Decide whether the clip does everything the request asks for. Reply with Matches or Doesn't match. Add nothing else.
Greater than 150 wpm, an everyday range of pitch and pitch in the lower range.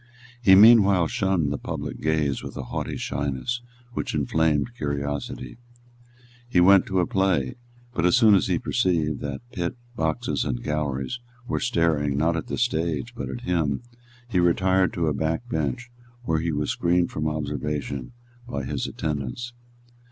Matches